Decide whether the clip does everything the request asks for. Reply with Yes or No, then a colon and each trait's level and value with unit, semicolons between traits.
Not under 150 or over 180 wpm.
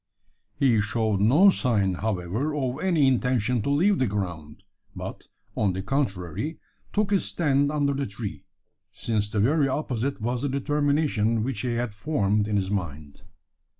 Yes: average, 155 wpm